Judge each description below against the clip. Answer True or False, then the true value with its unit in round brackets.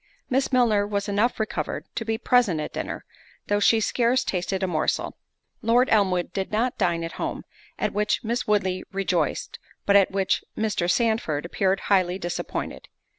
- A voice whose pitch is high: True (205 Hz)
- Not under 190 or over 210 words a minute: False (165 wpm)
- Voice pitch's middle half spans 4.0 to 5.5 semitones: False (3.5 semitones)